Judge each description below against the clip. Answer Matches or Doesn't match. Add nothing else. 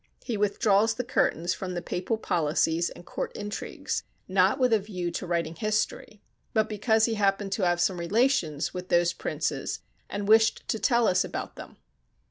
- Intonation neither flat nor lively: Matches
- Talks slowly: Doesn't match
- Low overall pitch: Doesn't match